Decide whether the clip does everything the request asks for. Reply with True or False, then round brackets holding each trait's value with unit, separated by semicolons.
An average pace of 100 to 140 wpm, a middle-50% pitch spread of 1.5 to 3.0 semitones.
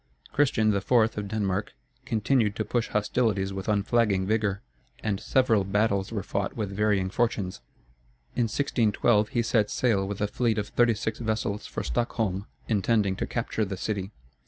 False (160 wpm; 2.5 semitones)